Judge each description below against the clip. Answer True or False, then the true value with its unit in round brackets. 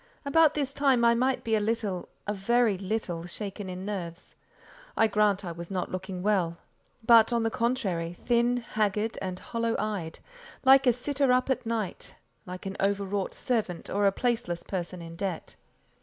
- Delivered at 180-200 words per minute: False (165 wpm)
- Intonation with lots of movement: False (4.2 semitones)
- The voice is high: True (210 Hz)